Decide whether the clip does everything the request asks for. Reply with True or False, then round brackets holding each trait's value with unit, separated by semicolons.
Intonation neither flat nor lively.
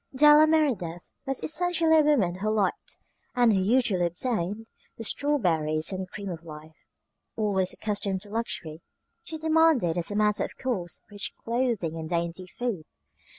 False (6.8 semitones)